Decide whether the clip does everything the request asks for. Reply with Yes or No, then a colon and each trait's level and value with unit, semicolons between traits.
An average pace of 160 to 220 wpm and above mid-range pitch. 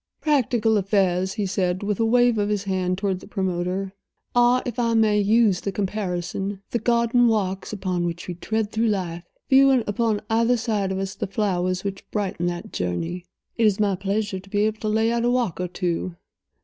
Yes: average, 200 wpm; high, 205 Hz